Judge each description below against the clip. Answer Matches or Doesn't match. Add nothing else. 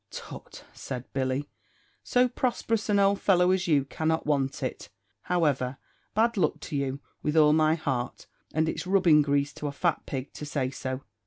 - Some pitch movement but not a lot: Matches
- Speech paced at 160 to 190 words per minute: Matches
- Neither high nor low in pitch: Matches